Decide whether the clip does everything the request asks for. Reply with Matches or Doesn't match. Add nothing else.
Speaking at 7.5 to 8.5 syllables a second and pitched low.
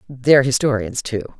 Doesn't match